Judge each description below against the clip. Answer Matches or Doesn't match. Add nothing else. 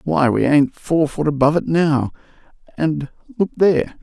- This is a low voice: Doesn't match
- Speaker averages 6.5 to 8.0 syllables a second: Doesn't match